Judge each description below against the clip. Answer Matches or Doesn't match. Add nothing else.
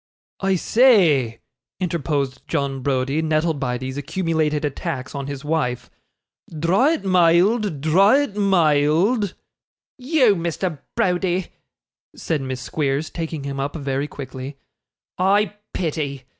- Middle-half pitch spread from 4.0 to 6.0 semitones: Matches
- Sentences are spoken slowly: Matches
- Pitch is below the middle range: Doesn't match